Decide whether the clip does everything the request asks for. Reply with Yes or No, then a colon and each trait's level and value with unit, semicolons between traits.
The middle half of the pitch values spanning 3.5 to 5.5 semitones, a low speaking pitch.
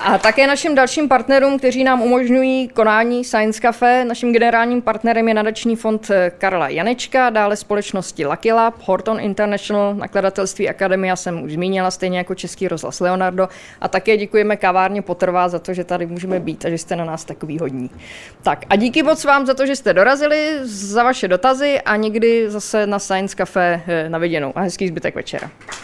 No: average, 4.4 semitones; high, 205 Hz